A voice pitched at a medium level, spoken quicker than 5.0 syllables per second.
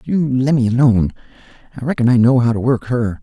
No: low, 120 Hz; 6.1 syllables/s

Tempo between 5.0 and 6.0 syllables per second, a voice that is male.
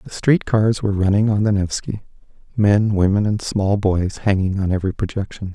Yes: 5.3 syllables/s; male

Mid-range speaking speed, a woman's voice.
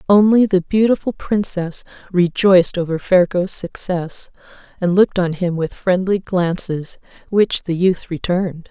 No: slow, 130 wpm; female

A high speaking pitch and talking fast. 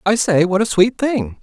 Yes: high, 195 Hz; fast, 250 wpm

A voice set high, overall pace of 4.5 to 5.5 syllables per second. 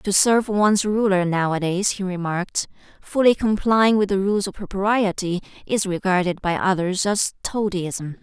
Yes: high, 195 Hz; 4.7 syllables/s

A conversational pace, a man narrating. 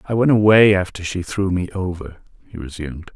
Yes: average, 190 wpm; male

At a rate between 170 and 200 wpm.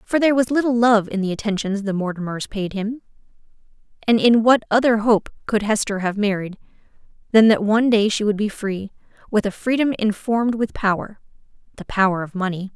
Yes: average, 185 wpm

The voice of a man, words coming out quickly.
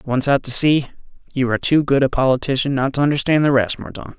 Yes: male; fast, 230 wpm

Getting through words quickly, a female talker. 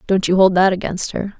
Yes: fast, 260 wpm; female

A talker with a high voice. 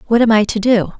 Yes: high, 215 Hz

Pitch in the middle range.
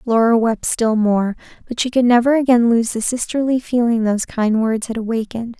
No: high, 230 Hz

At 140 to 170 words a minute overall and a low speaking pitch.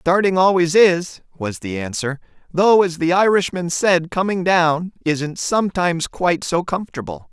No: average, 150 wpm; medium, 170 Hz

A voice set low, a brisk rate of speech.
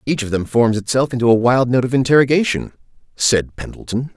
No: low, 125 Hz; average, 190 wpm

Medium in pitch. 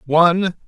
Yes: medium, 170 Hz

